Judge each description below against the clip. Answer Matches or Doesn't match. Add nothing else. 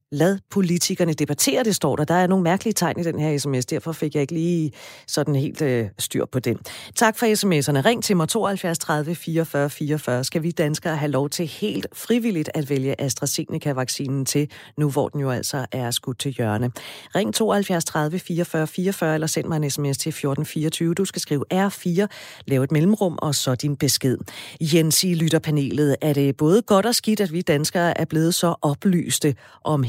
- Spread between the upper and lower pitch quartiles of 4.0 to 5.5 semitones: Doesn't match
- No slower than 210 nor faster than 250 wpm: Doesn't match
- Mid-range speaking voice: Matches